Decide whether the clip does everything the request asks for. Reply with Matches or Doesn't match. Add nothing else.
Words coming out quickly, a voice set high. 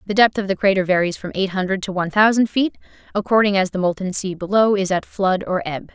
Matches